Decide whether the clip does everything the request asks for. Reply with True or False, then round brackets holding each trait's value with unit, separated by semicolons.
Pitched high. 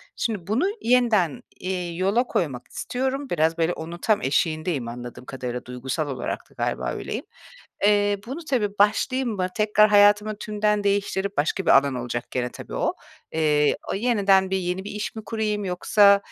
True (195 Hz)